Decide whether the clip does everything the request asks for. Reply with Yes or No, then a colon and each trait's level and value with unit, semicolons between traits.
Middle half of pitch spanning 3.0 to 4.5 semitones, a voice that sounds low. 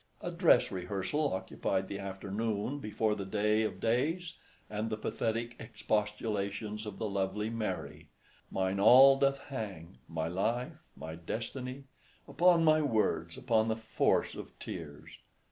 Yes: average, 3.9 semitones; low, 110 Hz